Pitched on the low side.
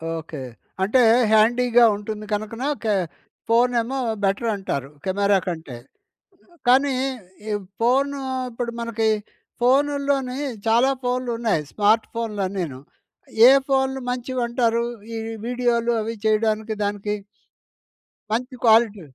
No: high, 230 Hz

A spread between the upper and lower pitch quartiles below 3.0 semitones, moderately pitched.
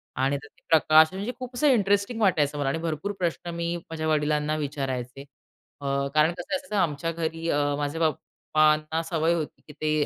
Yes: narrow, 2.5 semitones; medium, 160 Hz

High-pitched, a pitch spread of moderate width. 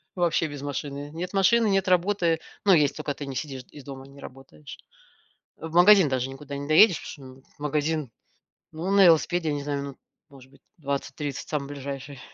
No: medium, 145 Hz; average, 3.5 semitones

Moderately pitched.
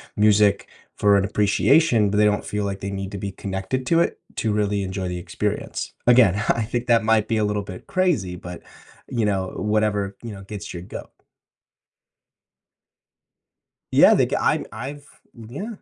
No: low, 105 Hz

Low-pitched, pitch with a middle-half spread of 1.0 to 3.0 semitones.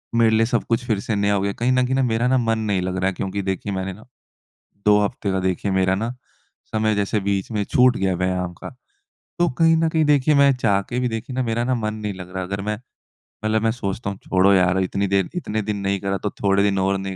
No: low, 105 Hz; average, 3.6 semitones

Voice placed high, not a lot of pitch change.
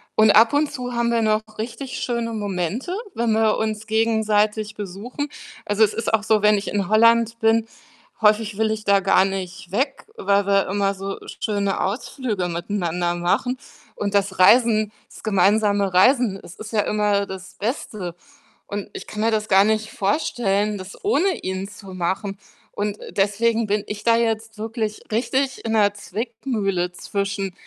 Yes: high, 210 Hz; narrow, 2.3 semitones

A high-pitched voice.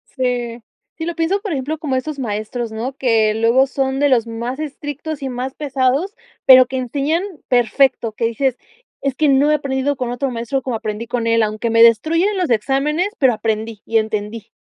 Yes: very high, 255 Hz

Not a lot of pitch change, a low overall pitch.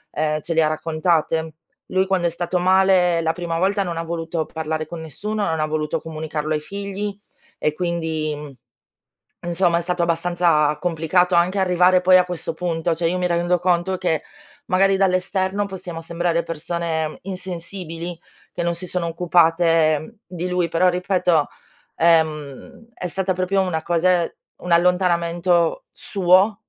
No: narrow, 2.0 semitones; medium, 170 Hz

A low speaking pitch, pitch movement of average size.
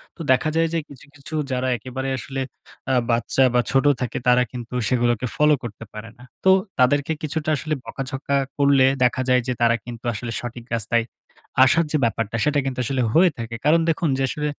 Yes: low, 130 Hz; average, 3.2 semitones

